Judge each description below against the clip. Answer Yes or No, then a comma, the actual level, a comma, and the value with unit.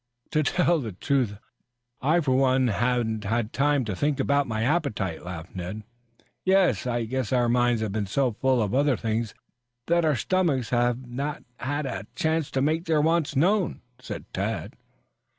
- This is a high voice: No, low, 130 Hz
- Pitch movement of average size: Yes, average, 4.9 semitones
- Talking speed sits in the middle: Yes, average, 170 wpm